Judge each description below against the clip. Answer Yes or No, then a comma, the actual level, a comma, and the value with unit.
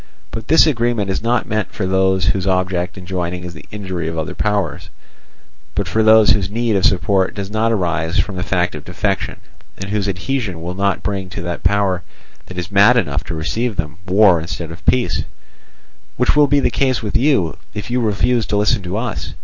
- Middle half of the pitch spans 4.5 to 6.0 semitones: No, average, 3.6 semitones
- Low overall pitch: Yes, very low, 95 Hz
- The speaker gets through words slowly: No, fast, 205 wpm